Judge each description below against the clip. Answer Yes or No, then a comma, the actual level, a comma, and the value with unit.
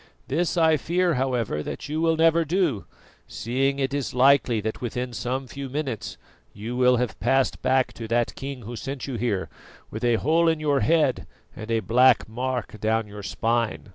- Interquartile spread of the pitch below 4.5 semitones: Yes, average, 3.6 semitones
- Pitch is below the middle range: Yes, low, 130 Hz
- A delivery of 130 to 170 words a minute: No, average, 185 wpm